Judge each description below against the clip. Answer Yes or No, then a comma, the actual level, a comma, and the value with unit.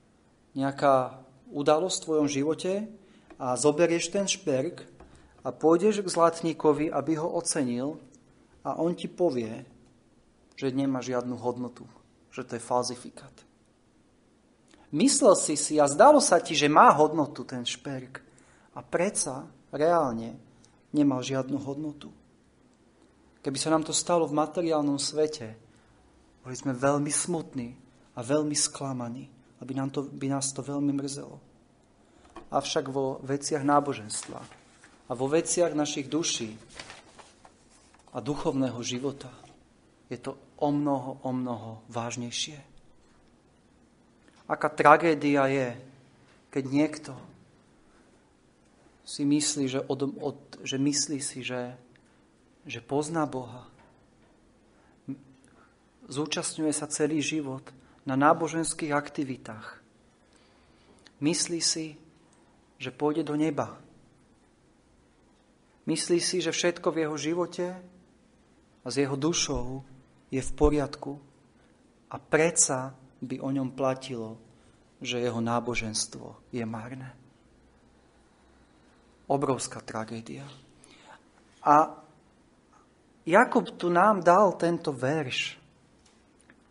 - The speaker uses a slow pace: Yes, slow, 105 wpm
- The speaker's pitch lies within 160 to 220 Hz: No, medium, 140 Hz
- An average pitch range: Yes, average, 3.6 semitones